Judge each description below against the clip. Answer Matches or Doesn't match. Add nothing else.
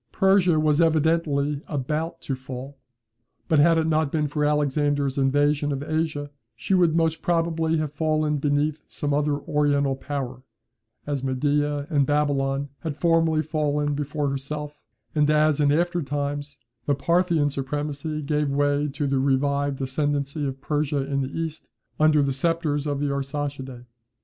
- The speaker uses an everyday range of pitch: Doesn't match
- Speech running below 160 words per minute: Matches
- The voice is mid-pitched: Matches